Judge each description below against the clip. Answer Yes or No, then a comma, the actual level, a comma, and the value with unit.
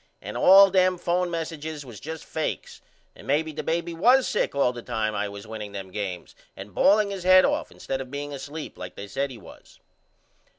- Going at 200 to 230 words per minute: Yes, fast, 205 wpm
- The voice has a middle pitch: Yes, medium, 145 Hz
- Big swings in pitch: Yes, wide, 7.9 semitones